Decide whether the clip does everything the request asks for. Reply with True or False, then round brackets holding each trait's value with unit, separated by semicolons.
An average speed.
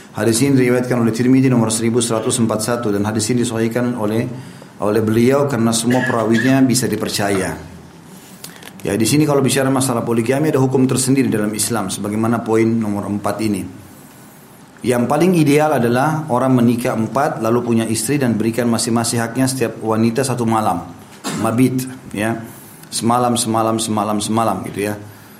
False (145 wpm)